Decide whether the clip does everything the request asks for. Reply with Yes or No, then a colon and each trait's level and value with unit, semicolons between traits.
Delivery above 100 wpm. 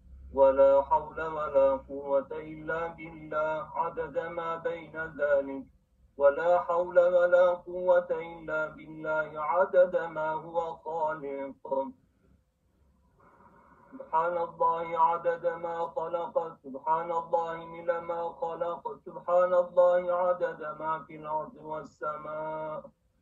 No: slow, 95 wpm